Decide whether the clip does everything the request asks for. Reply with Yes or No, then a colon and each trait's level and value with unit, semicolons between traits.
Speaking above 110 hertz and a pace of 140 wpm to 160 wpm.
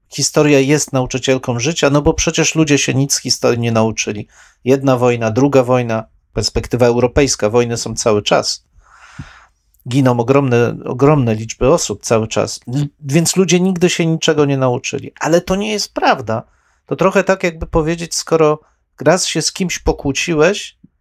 Yes: medium, 140 Hz; average, 155 wpm